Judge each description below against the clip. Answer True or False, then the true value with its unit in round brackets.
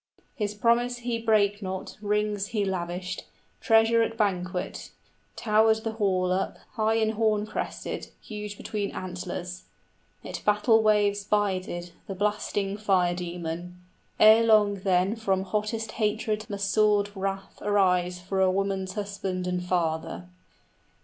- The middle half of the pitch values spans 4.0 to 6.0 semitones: False (2.5 semitones)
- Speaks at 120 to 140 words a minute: True (135 wpm)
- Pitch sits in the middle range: False (205 Hz)